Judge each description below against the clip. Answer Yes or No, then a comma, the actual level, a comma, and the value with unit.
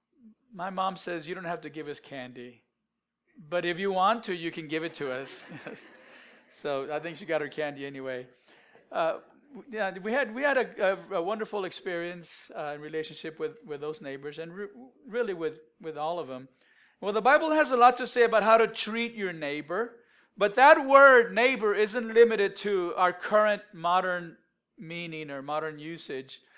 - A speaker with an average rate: Yes, average, 185 wpm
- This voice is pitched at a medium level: Yes, medium, 180 Hz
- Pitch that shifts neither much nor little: No, wide, 6.4 semitones